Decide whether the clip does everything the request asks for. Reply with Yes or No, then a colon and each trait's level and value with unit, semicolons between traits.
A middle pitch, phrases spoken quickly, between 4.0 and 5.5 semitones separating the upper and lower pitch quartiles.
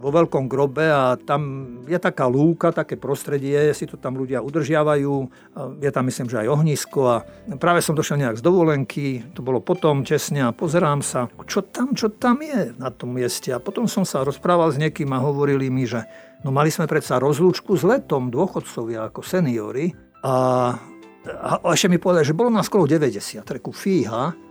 Yes: medium, 145 Hz; fast, 190 wpm; average, 4.7 semitones